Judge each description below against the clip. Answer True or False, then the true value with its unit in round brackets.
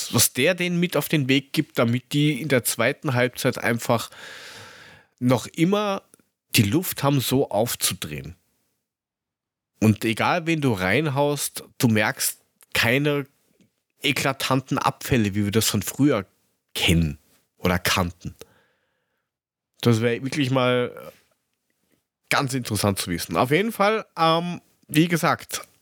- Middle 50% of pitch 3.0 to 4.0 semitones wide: False (5.1 semitones)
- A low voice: True (130 Hz)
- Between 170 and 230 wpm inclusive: False (125 wpm)